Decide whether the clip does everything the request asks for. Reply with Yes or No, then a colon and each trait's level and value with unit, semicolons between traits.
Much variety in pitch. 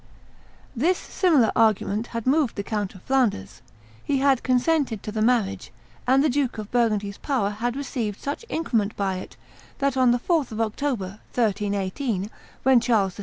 No: average, 4.5 semitones